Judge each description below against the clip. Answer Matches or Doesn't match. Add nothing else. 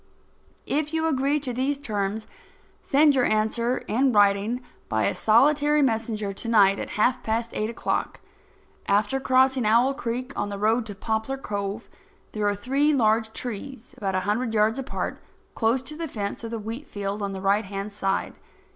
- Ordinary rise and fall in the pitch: Matches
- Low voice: Doesn't match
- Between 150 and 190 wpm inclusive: Matches